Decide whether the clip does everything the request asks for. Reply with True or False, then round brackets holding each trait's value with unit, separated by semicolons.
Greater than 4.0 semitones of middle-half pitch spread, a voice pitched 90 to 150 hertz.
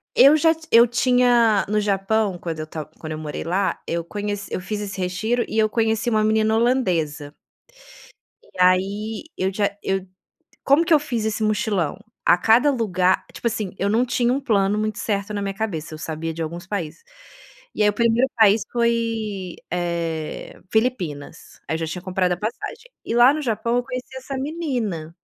False (4.5 semitones; 210 Hz)